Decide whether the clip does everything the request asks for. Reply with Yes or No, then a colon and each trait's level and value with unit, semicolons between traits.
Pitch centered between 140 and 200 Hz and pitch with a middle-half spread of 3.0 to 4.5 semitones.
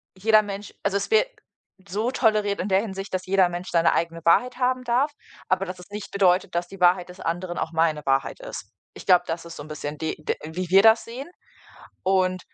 Yes: medium, 185 Hz; average, 3.4 semitones